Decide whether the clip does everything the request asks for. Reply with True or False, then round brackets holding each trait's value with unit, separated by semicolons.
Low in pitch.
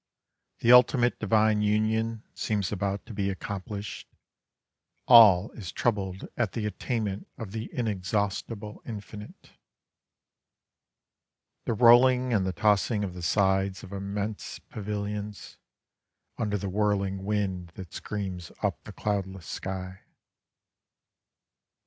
True (105 Hz)